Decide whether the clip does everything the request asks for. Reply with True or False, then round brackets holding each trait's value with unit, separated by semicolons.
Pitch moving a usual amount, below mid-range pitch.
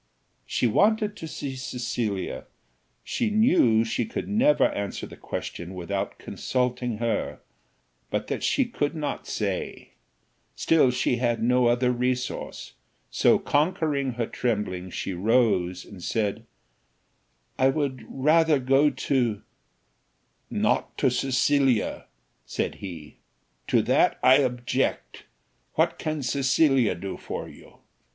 True (4.7 semitones; 125 Hz)